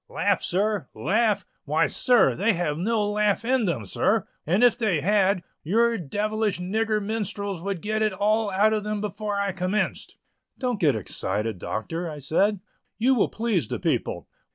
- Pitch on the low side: No, high, 205 Hz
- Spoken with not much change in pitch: No, average, 3.7 semitones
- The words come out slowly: No, average, 170 wpm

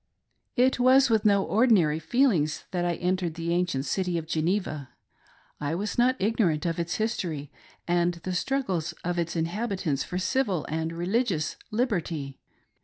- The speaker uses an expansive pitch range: No, average, 4.9 semitones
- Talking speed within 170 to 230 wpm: No, average, 150 wpm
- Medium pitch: Yes, medium, 175 Hz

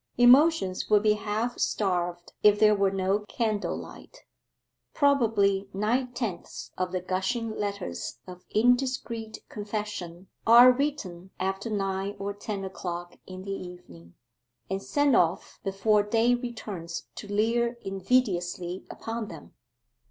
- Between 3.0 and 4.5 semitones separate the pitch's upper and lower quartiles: Yes, average, 3.6 semitones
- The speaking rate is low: Yes, slow, 125 wpm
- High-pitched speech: Yes, high, 205 Hz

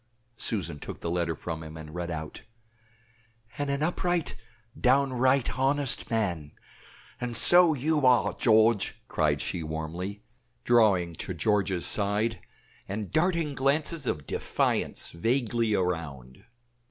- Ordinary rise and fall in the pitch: No, wide, 7.9 semitones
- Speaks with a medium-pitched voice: No, low, 110 Hz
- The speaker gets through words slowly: Yes, slow, 120 wpm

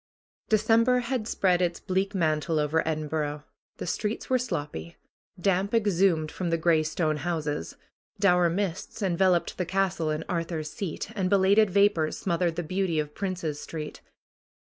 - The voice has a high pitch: No, medium, 175 Hz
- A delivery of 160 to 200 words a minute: No, average, 150 wpm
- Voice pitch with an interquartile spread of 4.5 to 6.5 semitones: No, average, 3.8 semitones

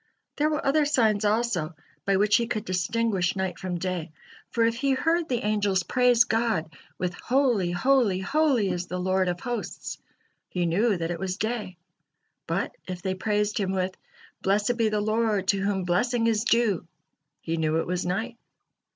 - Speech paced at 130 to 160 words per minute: No, average, 175 wpm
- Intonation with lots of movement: No, average, 4.3 semitones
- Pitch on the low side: No, high, 205 Hz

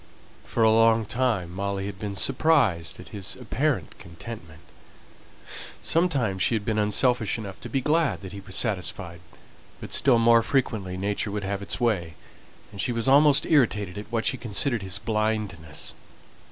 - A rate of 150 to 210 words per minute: Yes, average, 165 wpm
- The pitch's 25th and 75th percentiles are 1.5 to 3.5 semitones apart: No, average, 3.9 semitones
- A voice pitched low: Yes, low, 110 Hz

